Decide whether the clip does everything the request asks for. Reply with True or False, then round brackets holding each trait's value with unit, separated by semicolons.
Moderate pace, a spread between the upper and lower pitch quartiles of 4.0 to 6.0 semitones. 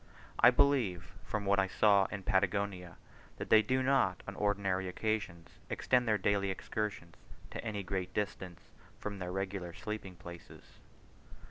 False (145 wpm; 2.5 semitones)